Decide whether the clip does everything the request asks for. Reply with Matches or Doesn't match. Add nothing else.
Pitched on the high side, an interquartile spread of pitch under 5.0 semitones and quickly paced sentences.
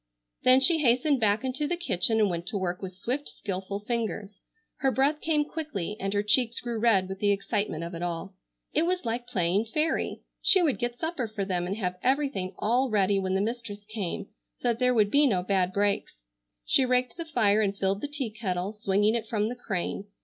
Matches